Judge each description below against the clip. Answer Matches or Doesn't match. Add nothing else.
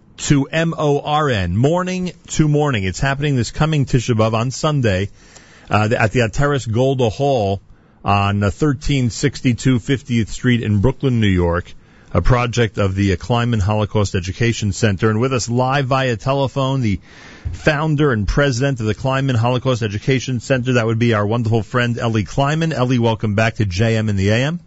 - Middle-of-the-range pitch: Doesn't match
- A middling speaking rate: Matches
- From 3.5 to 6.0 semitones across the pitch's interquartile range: Matches